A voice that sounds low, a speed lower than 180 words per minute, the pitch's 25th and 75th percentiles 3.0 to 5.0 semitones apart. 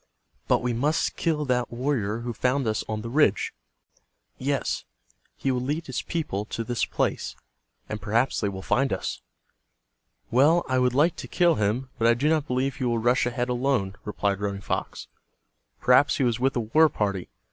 No: low, 125 Hz; average, 185 wpm; average, 3.8 semitones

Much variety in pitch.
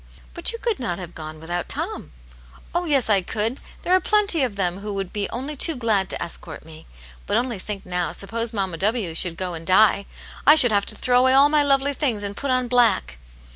Yes: wide, 6.6 semitones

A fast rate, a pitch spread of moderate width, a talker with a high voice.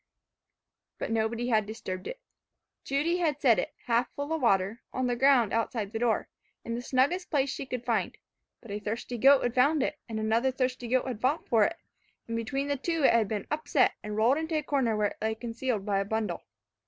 Yes: fast, 215 wpm; average, 3.9 semitones; high, 245 Hz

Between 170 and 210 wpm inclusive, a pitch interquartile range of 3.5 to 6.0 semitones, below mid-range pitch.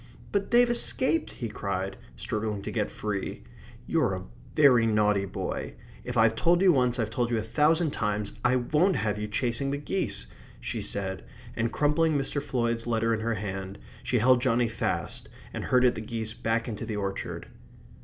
Yes: average, 180 wpm; average, 4.3 semitones; low, 115 Hz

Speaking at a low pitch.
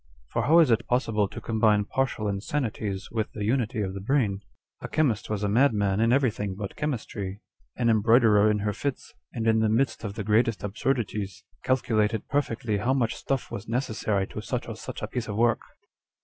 Yes: low, 110 Hz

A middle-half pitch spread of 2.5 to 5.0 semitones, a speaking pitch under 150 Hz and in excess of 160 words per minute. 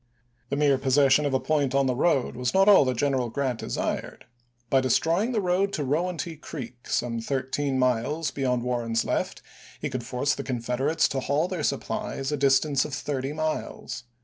Yes: average, 3.0 semitones; low, 135 Hz; average, 185 wpm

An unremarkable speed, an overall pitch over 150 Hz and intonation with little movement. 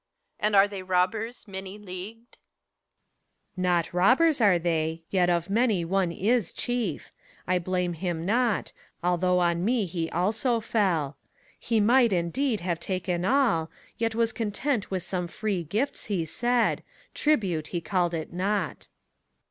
No: average, 150 wpm; high, 190 Hz; average, 4.5 semitones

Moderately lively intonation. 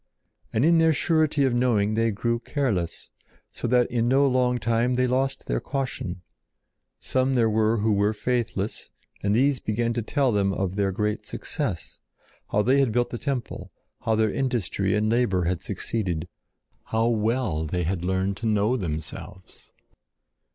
Yes: average, 3.9 semitones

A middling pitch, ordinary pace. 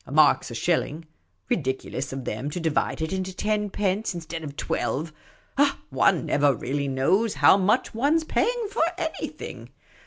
Yes: medium, 170 Hz; average, 175 wpm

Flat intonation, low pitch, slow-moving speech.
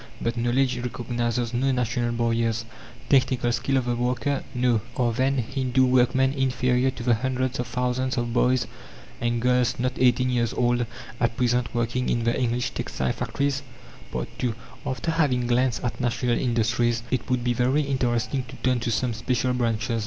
No: narrow, 1.4 semitones; low, 125 Hz; average, 165 wpm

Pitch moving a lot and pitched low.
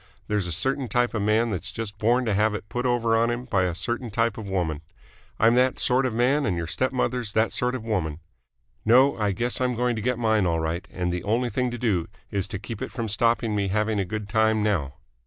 No: average, 3.5 semitones; low, 110 Hz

